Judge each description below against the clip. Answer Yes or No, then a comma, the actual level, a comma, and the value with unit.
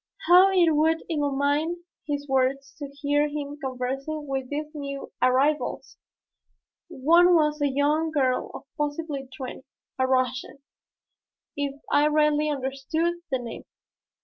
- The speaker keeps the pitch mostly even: Yes, narrow, 2.2 semitones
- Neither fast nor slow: No, slow, 125 wpm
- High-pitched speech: Yes, very high, 290 Hz